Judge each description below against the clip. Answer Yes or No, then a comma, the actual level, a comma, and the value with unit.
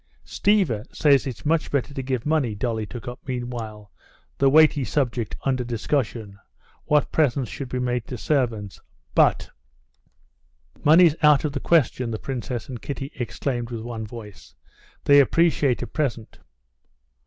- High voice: No, low, 125 Hz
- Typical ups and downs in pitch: Yes, average, 3.7 semitones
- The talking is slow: No, average, 145 wpm